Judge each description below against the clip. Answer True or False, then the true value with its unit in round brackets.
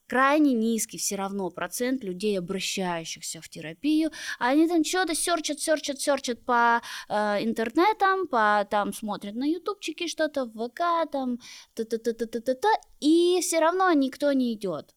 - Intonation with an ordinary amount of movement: False (7.3 semitones)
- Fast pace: False (135 wpm)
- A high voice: True (255 Hz)